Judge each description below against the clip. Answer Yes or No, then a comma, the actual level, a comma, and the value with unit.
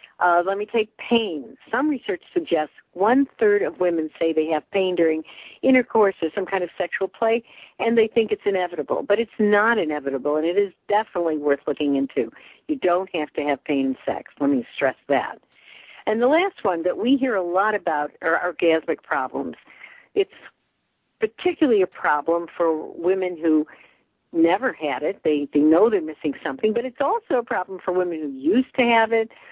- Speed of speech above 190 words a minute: Yes, average, 200 wpm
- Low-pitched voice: No, high, 190 Hz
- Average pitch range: No, wide, 6.3 semitones